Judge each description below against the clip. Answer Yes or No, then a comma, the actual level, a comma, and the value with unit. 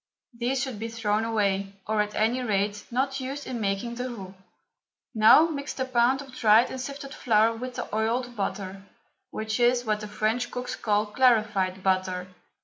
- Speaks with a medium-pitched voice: No, high, 225 Hz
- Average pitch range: Yes, average, 3.3 semitones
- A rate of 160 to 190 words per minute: Yes, average, 175 wpm